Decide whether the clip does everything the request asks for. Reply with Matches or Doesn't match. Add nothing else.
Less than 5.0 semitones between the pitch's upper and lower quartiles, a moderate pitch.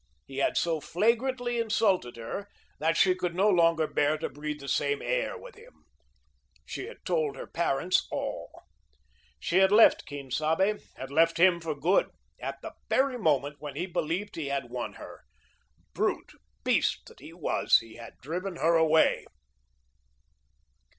Doesn't match